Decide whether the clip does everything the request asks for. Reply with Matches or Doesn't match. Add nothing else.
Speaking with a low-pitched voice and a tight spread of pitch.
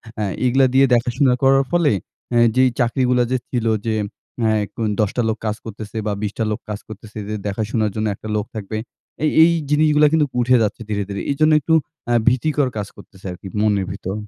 Doesn't match